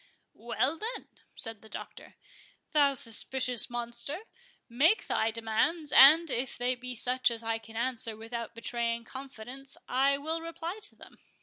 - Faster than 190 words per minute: No, average, 145 wpm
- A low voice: No, very high, 250 Hz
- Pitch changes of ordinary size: Yes, average, 3.5 semitones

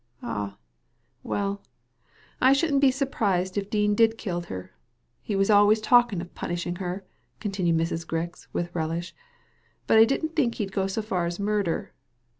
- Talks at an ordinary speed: Yes, average, 165 wpm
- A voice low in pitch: No, high, 195 Hz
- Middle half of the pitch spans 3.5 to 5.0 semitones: Yes, average, 4.2 semitones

